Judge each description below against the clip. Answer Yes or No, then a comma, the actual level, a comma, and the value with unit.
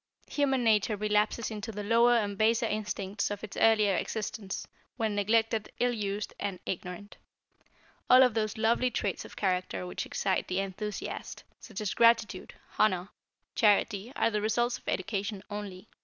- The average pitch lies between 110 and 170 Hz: No, high, 210 Hz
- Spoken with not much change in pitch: Yes, narrow, 2.2 semitones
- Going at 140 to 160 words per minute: Yes, average, 155 wpm